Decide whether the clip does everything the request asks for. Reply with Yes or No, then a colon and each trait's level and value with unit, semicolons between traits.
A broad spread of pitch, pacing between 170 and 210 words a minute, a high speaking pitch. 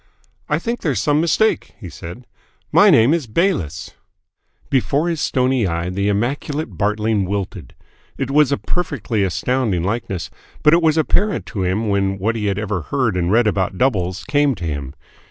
No: wide, 7.0 semitones; average, 175 wpm; low, 110 Hz